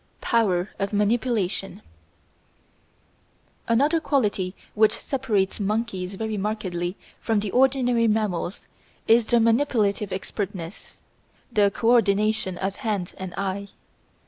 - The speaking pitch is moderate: No, high, 210 Hz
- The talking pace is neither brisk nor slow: No, slow, 100 wpm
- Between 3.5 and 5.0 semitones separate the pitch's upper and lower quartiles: No, average, 3.1 semitones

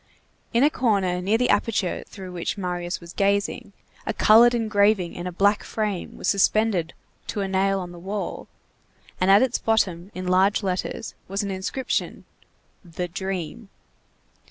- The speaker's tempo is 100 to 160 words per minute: Yes, average, 155 wpm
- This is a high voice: Yes, high, 195 Hz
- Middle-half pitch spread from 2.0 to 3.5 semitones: Yes, average, 2.9 semitones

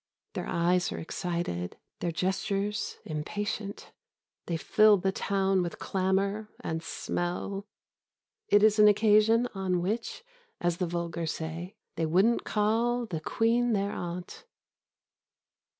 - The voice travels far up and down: No, average, 3.5 semitones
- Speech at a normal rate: No, slow, 120 wpm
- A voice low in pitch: No, high, 195 Hz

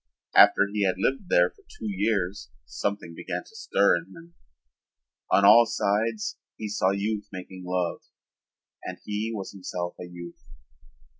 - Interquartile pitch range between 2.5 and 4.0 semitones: Yes, average, 2.9 semitones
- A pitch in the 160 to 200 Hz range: No, low, 100 Hz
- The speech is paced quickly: No, average, 150 wpm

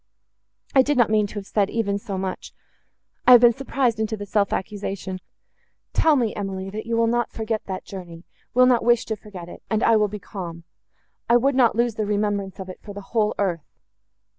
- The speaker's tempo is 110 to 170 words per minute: No, fast, 205 wpm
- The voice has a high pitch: Yes, high, 210 Hz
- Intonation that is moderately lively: Yes, average, 3.1 semitones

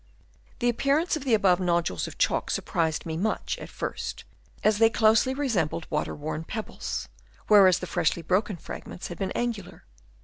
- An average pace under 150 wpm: No, average, 165 wpm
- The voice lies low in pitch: No, high, 195 Hz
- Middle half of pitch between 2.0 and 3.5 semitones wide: No, average, 4.9 semitones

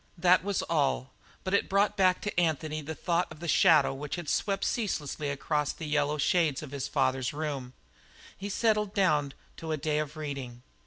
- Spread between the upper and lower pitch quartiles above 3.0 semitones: Yes, average, 4.2 semitones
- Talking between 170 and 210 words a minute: Yes, average, 195 wpm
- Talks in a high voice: No, medium, 155 Hz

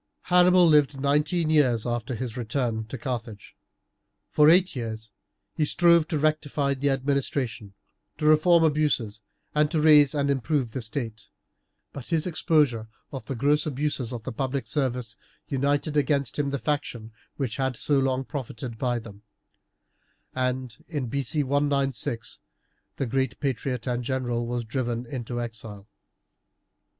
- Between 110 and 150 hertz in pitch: Yes, low, 135 Hz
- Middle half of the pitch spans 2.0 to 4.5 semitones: Yes, average, 3.8 semitones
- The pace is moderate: Yes, average, 145 wpm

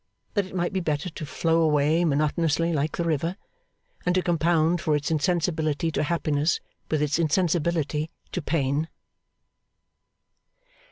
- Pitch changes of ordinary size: No, narrow, 2.3 semitones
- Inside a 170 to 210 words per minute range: No, slow, 135 wpm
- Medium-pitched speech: Yes, medium, 160 Hz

